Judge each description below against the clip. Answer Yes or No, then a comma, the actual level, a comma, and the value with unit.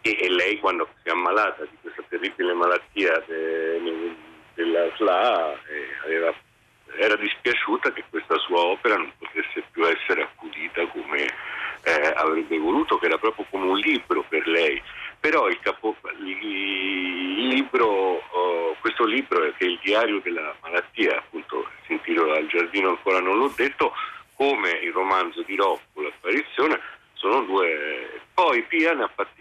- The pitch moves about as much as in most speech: No, wide, 5.7 semitones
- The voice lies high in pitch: Yes, very high, 370 Hz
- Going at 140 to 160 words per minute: Yes, average, 155 wpm